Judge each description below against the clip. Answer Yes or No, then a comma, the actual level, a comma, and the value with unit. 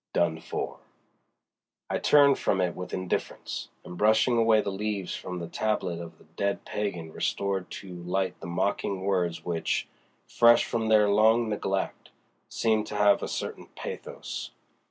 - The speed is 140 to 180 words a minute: Yes, average, 155 wpm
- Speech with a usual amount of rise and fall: Yes, average, 3.4 semitones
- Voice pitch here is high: No, low, 100 Hz